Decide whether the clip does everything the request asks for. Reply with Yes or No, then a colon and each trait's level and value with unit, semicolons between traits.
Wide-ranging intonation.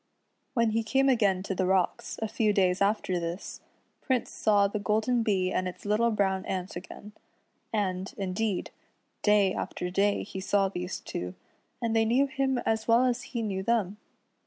No: average, 3.1 semitones